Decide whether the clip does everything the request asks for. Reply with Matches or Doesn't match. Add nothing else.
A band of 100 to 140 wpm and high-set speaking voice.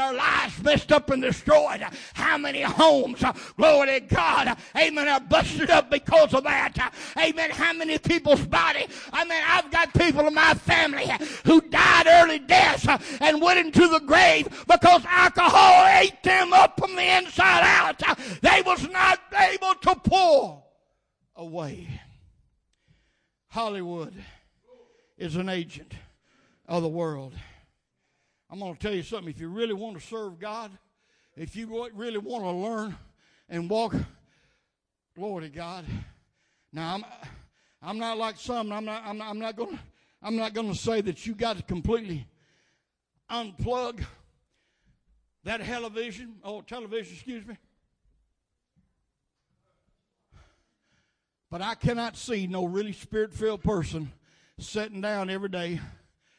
Matches